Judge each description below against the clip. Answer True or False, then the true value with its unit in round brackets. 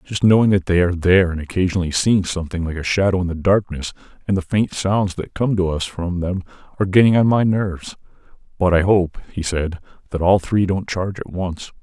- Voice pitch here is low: True (90 Hz)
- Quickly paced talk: True (220 wpm)